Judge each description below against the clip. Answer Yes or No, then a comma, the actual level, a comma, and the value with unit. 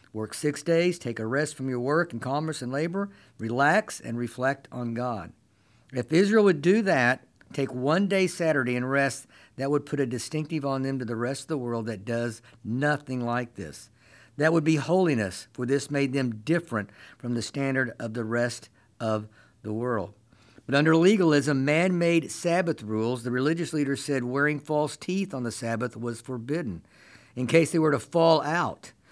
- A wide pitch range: No, average, 4.8 semitones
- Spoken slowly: No, average, 190 wpm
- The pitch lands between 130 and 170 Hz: Yes, low, 135 Hz